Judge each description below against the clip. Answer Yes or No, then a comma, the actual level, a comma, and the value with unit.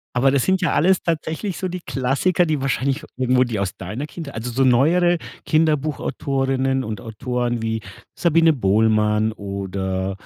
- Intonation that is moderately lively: No, wide, 5.9 semitones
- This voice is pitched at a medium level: No, low, 130 Hz